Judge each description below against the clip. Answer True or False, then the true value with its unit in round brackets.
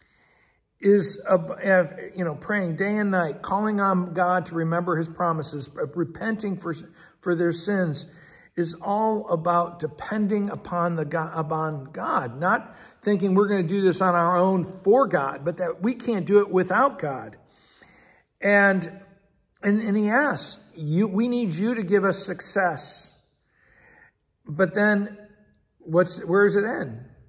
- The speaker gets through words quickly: False (150 wpm)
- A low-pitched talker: False (185 Hz)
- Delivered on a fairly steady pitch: False (3.2 semitones)